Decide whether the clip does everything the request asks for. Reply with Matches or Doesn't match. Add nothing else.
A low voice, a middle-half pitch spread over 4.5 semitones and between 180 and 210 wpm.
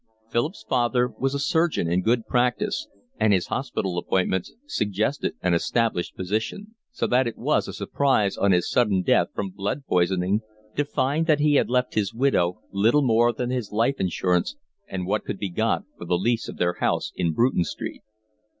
Matches